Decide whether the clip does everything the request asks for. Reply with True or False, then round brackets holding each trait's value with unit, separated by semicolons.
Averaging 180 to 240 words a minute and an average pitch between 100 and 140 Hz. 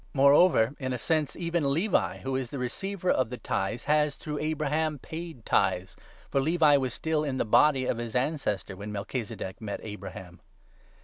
True (185 wpm; 135 Hz)